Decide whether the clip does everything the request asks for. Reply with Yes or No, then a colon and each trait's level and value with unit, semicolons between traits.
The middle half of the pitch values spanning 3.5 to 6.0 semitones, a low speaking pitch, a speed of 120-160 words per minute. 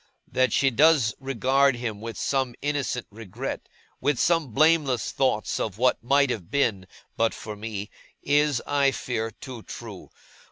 Yes: average, 3.8 semitones; low, 125 Hz; average, 150 wpm